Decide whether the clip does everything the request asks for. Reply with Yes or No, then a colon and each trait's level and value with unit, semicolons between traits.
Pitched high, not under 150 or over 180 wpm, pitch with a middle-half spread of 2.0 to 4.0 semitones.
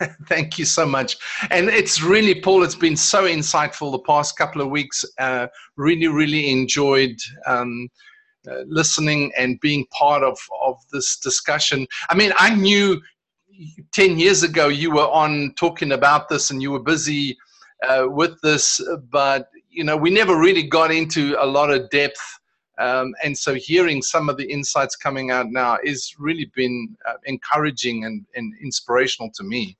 No: medium, 150 Hz; average, 170 wpm; average, 3.7 semitones